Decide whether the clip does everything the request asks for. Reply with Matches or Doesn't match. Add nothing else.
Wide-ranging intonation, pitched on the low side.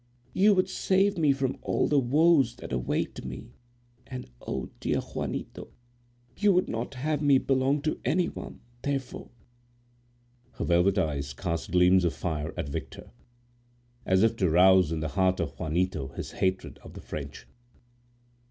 Matches